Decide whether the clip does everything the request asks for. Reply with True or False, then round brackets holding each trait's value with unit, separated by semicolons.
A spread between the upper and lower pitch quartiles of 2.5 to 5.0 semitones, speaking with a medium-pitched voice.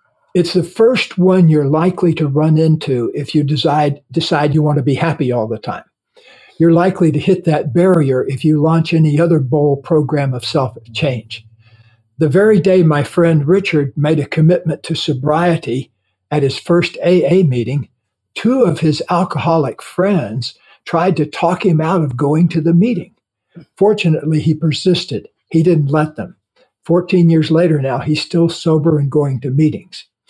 True (2.9 semitones; 155 Hz)